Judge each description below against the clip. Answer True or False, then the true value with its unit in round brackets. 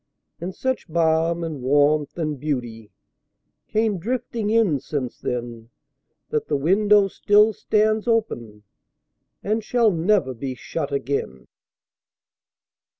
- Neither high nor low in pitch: True (160 Hz)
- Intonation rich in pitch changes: True (7.6 semitones)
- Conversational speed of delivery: False (95 wpm)